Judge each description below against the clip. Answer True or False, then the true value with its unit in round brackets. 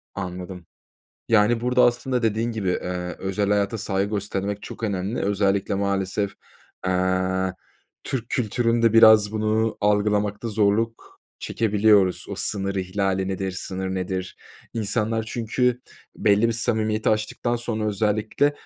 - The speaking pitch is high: False (105 Hz)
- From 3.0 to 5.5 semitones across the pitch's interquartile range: False (2.6 semitones)